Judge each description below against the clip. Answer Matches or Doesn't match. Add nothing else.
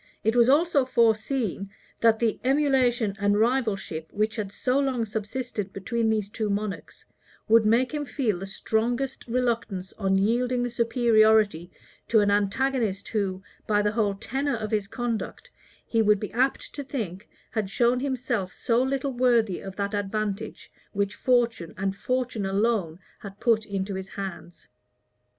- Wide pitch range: Doesn't match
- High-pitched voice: Matches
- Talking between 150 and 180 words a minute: Matches